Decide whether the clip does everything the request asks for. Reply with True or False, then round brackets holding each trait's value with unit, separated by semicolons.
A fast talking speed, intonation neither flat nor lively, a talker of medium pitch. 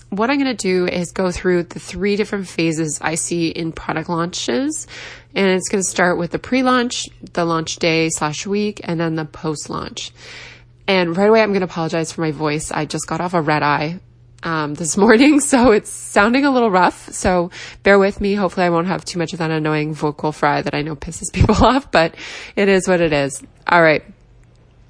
True (220 wpm; 3.9 semitones; 175 Hz)